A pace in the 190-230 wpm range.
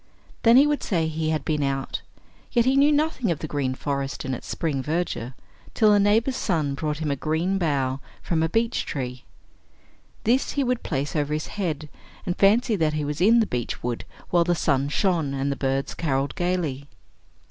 Yes: average, 200 wpm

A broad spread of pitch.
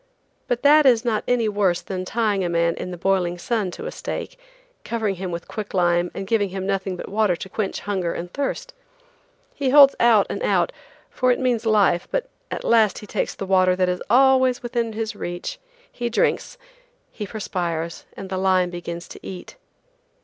No: average, 4.5 semitones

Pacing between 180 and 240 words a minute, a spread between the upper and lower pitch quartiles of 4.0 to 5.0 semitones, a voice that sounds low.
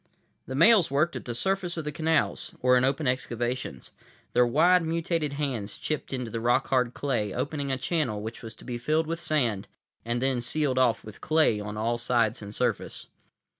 Yes: average, 195 wpm; average, 4.6 semitones; low, 130 Hz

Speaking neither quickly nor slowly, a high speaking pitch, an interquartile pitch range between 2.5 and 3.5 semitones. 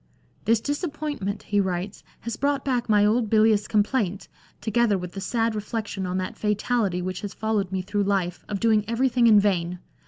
Yes: average, 195 wpm; high, 210 Hz; average, 3.1 semitones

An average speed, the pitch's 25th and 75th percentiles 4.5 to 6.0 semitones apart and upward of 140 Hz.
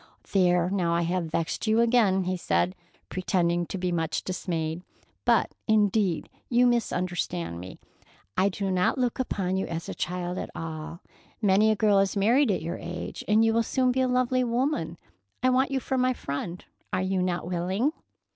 Yes: average, 185 wpm; average, 4.8 semitones; medium, 185 Hz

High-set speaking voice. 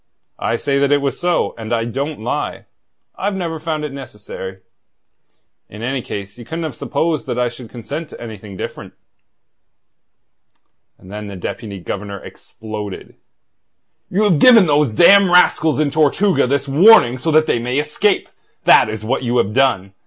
No: low, 135 Hz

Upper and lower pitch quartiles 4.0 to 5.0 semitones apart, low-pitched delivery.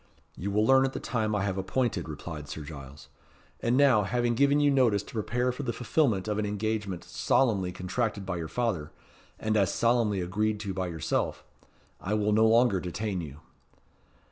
Yes: average, 4.3 semitones; low, 105 Hz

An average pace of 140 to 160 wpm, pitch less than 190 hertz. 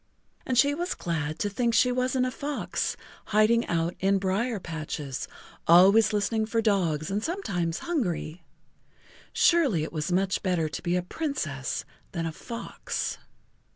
No: average, 150 wpm; high, 195 Hz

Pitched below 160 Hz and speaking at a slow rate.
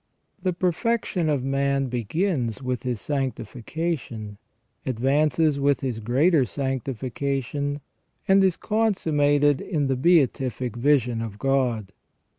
Yes: low, 135 Hz; slow, 110 wpm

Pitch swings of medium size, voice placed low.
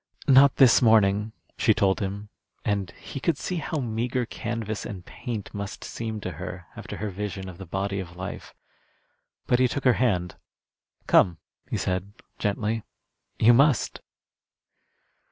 Yes: average, 3.9 semitones; low, 105 Hz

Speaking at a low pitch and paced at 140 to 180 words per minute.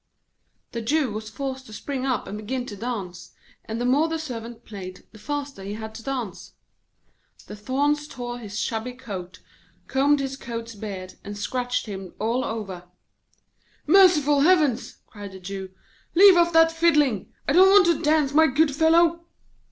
No: very high, 250 Hz; average, 165 wpm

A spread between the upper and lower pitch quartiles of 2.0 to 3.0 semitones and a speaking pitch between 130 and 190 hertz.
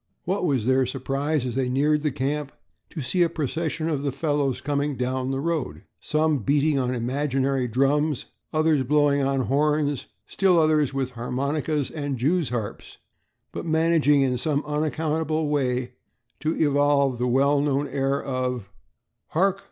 Yes: average, 2.7 semitones; medium, 140 Hz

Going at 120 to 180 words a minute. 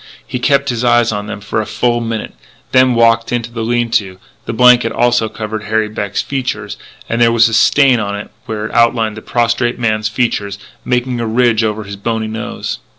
No: fast, 205 wpm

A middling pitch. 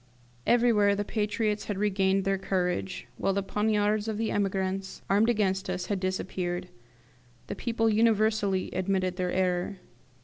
No: high, 195 Hz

